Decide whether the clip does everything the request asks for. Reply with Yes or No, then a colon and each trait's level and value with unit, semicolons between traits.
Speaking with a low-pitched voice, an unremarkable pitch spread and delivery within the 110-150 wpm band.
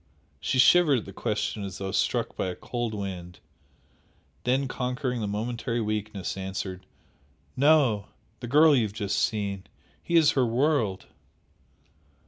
Yes: low, 110 Hz; average, 4.6 semitones; average, 140 wpm